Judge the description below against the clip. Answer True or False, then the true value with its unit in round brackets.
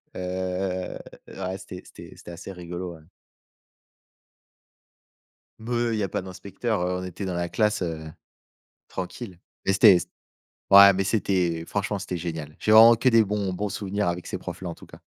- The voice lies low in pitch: True (95 Hz)